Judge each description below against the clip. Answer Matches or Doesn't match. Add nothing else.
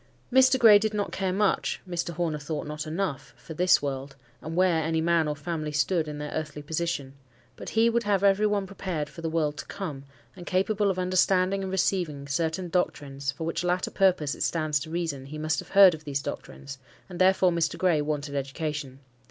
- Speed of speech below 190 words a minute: Doesn't match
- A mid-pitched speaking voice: Matches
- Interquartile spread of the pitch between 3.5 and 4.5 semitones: Matches